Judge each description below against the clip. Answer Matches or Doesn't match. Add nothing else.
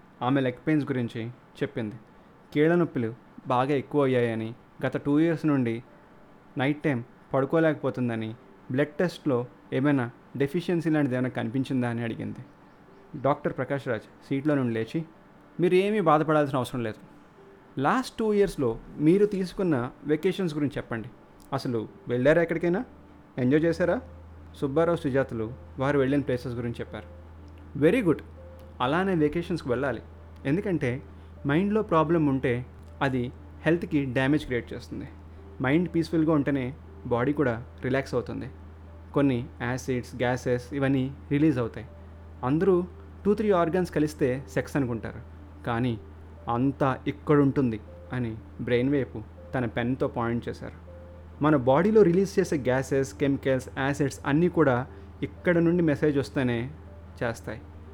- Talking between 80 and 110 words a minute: Doesn't match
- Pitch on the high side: Doesn't match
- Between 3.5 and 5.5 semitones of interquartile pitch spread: Matches